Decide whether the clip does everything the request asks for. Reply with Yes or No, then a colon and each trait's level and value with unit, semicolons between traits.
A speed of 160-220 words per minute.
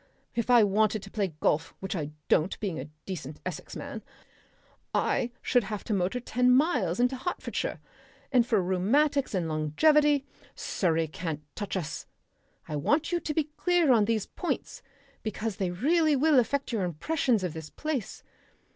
Yes: average, 165 wpm